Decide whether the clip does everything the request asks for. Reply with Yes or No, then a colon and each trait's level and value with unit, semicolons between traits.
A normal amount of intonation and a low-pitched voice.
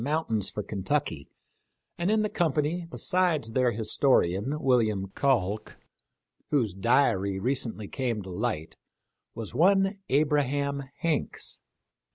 No: wide, 6.0 semitones; low, 130 Hz